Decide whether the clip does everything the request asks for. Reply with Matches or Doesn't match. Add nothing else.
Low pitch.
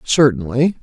Matches